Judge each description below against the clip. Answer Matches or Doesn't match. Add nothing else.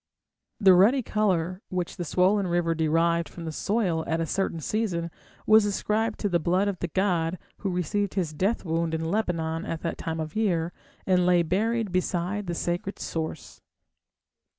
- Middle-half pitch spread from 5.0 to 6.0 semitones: Doesn't match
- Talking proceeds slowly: Doesn't match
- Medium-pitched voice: Matches